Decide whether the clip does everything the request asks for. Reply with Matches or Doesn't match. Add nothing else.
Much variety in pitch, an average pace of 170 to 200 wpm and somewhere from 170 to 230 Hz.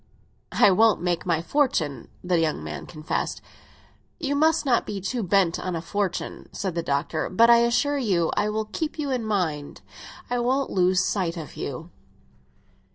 Matches